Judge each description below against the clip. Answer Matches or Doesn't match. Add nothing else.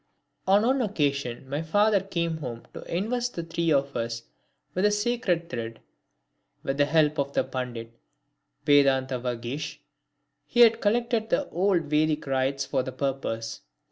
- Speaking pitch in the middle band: Matches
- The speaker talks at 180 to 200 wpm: Doesn't match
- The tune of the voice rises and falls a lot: Matches